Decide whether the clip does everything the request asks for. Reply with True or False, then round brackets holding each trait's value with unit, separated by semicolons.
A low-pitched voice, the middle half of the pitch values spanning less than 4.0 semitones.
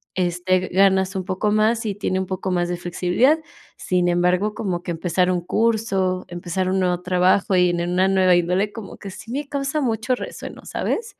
False (185 Hz; 2.9 semitones)